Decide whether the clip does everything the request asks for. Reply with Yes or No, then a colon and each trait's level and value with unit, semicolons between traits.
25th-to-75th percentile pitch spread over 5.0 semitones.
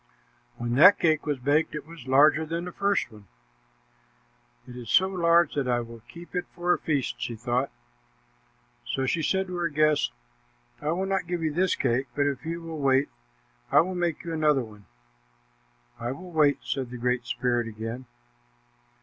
Yes: wide, 5.4 semitones